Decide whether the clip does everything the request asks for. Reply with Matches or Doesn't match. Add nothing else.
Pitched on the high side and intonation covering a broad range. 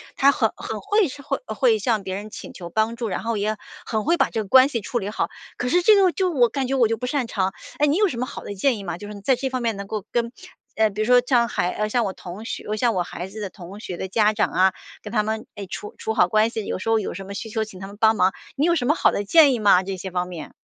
Doesn't match